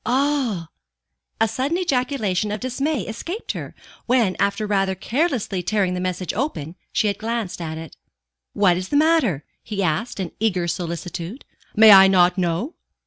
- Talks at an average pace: Yes, average, 155 wpm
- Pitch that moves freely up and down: Yes, wide, 5.7 semitones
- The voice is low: No, high, 205 Hz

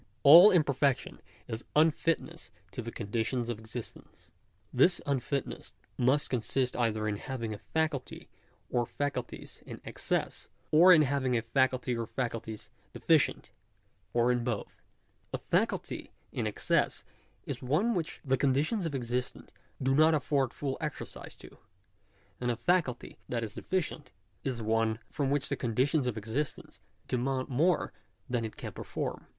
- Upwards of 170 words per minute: No, average, 145 wpm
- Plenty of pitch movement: No, average, 3.9 semitones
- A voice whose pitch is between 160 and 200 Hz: No, low, 130 Hz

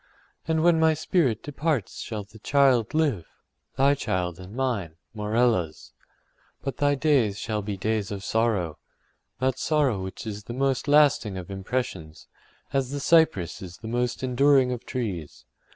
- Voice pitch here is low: Yes, low, 120 Hz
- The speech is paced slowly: No, average, 145 wpm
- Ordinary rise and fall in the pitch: No, wide, 5.8 semitones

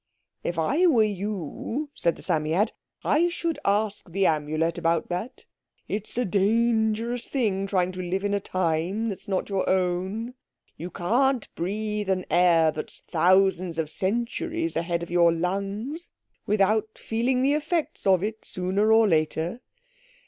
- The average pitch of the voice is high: Yes, high, 195 Hz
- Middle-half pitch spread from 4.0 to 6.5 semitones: Yes, average, 4.4 semitones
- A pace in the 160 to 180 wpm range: No, average, 150 wpm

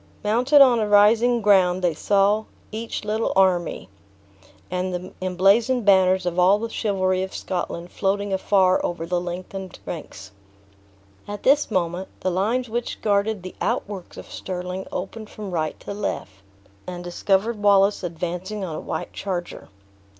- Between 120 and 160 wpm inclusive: Yes, average, 150 wpm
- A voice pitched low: No, high, 190 Hz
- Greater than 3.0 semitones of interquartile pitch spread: No, average, 2.7 semitones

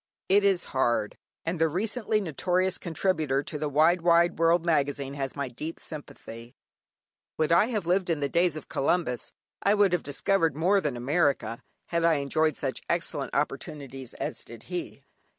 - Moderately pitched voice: Yes, medium, 160 Hz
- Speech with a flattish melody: No, average, 4.1 semitones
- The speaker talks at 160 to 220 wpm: Yes, average, 170 wpm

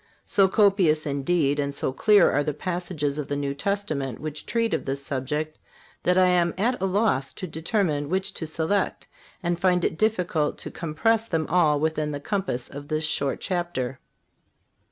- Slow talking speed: No, average, 175 wpm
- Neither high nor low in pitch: Yes, medium, 160 Hz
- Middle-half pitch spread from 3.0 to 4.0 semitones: No, average, 4.5 semitones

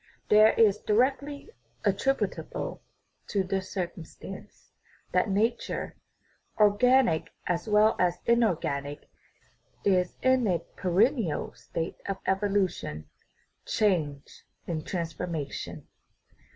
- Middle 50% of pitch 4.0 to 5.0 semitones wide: Yes, average, 4.3 semitones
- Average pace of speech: No, slow, 90 wpm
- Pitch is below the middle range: No, high, 195 Hz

